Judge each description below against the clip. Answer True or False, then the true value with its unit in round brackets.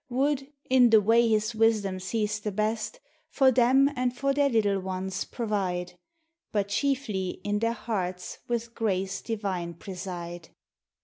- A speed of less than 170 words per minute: True (145 wpm)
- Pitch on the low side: False (215 Hz)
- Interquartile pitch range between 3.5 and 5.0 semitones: True (3.8 semitones)